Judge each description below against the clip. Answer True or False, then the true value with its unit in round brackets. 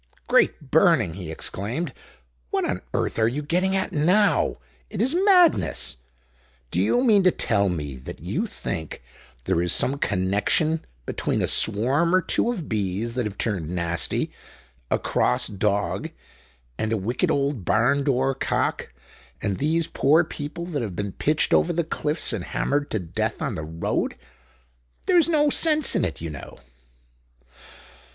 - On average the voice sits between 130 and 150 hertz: True (135 Hz)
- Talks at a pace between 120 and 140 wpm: False (160 wpm)